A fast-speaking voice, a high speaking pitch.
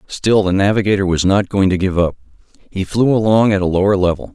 No: fast, 220 wpm; low, 100 Hz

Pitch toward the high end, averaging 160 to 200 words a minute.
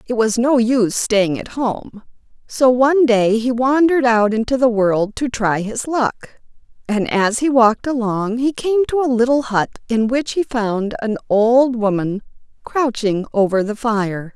Yes: high, 235 Hz; average, 175 wpm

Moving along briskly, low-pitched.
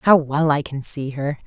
No: fast, 245 wpm; medium, 145 Hz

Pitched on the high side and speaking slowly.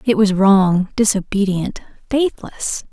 Yes: high, 205 Hz; slow, 105 wpm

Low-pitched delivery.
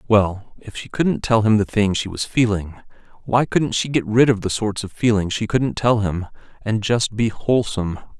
Yes: low, 110 Hz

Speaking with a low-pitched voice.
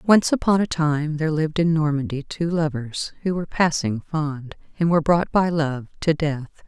No: medium, 155 Hz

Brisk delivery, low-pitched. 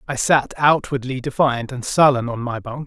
No: average, 190 wpm; low, 130 Hz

